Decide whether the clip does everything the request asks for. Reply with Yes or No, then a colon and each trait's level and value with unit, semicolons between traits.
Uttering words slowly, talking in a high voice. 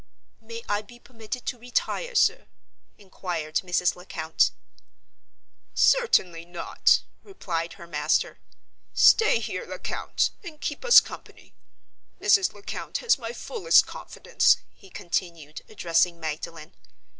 Yes: slow, 110 wpm; high, 200 Hz